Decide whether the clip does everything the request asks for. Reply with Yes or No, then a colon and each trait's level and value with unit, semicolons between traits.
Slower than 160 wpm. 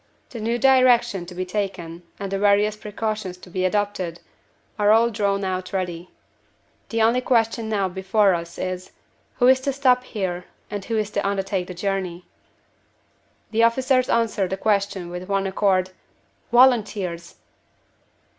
Yes: average, 150 wpm